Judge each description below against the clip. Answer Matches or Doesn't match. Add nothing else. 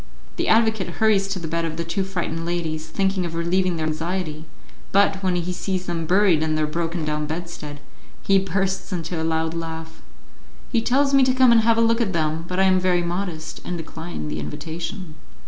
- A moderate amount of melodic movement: Matches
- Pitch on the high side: Doesn't match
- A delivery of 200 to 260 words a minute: Matches